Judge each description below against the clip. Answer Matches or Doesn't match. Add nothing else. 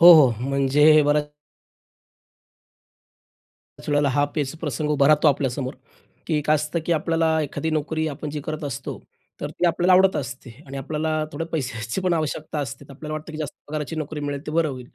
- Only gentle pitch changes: Matches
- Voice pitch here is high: Doesn't match